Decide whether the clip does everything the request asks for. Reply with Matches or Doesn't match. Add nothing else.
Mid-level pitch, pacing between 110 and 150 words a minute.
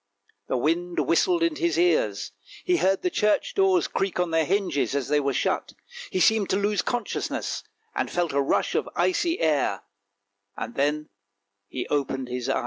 Doesn't match